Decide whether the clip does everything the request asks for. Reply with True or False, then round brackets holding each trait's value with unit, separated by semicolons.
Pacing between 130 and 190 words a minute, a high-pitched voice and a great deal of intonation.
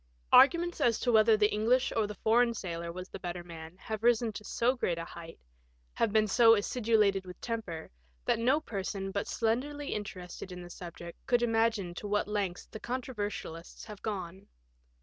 False (180 wpm; 210 Hz; 4.2 semitones)